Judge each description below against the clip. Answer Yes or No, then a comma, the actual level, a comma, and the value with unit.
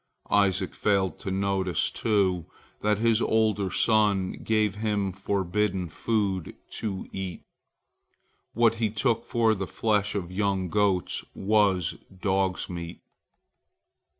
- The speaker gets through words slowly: Yes, slow, 115 wpm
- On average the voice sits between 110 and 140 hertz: No, low, 100 Hz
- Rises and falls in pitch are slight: Yes, narrow, 2.3 semitones